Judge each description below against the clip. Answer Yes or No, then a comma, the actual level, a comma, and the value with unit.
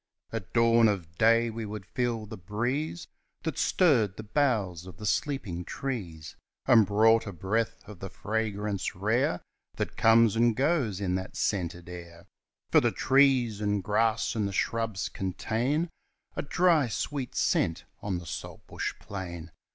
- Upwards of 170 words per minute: No, average, 150 wpm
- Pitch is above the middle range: No, low, 110 Hz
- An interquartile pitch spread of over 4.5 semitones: No, average, 3.8 semitones